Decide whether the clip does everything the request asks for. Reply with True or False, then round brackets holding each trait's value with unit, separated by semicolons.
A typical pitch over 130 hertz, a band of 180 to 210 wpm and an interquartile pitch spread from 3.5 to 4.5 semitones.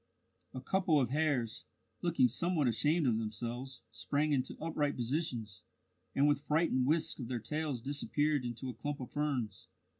False (140 Hz; 155 wpm; 4.0 semitones)